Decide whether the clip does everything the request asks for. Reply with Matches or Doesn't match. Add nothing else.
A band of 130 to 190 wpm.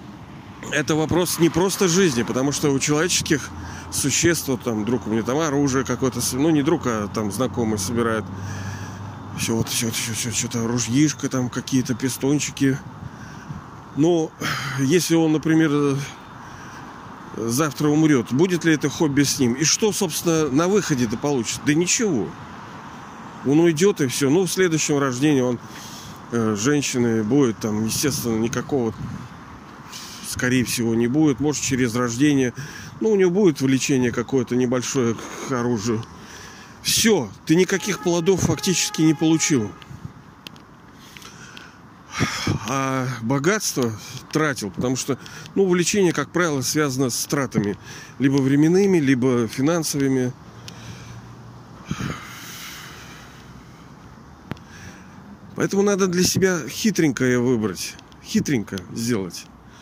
Doesn't match